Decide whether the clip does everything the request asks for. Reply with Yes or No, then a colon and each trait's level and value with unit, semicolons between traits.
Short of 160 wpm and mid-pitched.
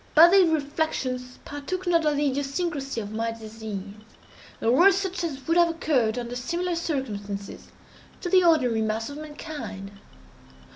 No: average, 150 wpm; very high, 285 Hz